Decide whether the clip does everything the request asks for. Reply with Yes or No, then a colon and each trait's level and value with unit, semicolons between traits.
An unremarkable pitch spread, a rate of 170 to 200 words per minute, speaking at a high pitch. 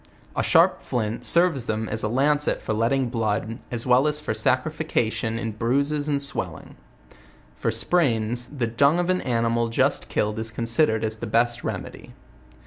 No: average, 4.1 semitones; average, 175 wpm; low, 120 Hz